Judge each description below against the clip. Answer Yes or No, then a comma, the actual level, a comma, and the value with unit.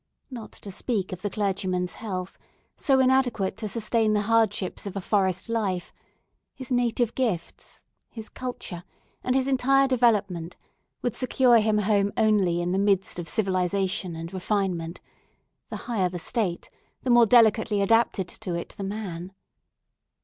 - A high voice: Yes, high, 205 Hz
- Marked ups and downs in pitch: No, average, 3.8 semitones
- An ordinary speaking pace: Yes, average, 150 wpm